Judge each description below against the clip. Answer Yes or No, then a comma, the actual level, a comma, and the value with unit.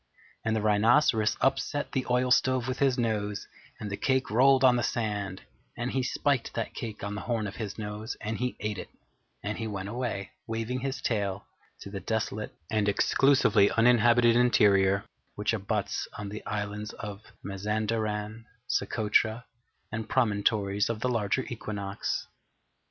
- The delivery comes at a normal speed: Yes, average, 155 wpm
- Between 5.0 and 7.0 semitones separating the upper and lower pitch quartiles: No, average, 2.8 semitones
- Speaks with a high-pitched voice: No, low, 110 Hz